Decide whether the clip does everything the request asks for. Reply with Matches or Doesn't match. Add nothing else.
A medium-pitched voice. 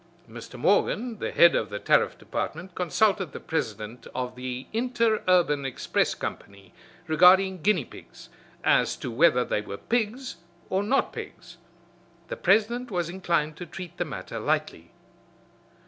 Matches